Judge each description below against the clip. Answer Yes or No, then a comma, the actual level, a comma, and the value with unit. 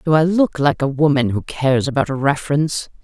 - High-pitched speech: No, medium, 145 Hz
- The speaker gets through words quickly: Yes, fast, 215 wpm